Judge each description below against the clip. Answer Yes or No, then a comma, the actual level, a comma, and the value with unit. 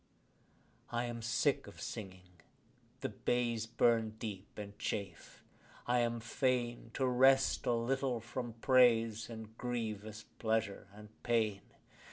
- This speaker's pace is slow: Yes, slow, 125 wpm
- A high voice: No, low, 115 Hz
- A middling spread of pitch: No, narrow, 2.1 semitones